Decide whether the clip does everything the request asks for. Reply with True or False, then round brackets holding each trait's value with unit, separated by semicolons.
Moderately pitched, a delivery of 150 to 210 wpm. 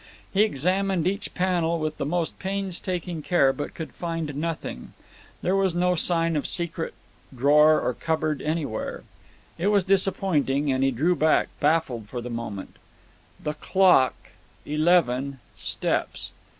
False (160 Hz; 135 wpm)